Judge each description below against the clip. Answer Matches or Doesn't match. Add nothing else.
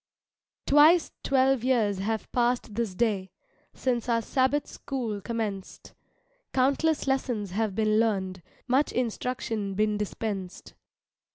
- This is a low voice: Doesn't match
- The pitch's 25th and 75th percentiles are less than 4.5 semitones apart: Matches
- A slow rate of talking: Matches